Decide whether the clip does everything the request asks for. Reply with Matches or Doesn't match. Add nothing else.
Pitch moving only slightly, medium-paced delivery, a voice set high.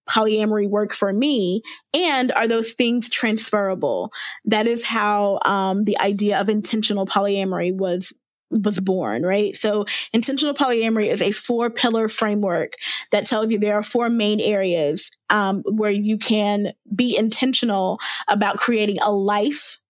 Matches